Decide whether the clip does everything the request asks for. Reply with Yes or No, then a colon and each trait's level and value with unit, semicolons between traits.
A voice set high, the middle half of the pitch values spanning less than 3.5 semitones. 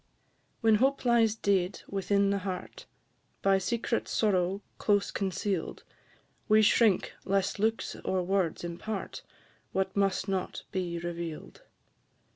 Yes: high, 195 Hz; narrow, 2.6 semitones